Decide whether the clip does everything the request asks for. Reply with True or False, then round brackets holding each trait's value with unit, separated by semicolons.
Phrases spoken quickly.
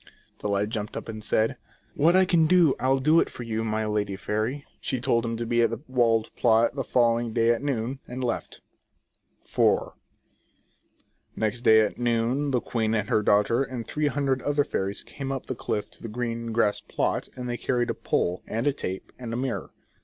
True (215 wpm)